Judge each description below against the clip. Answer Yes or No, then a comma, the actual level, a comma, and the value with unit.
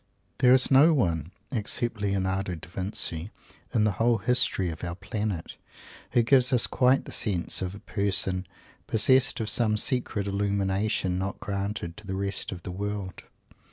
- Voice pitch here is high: No, low, 100 Hz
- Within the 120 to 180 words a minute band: Yes, average, 160 wpm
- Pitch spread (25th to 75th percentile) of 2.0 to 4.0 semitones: Yes, average, 3.3 semitones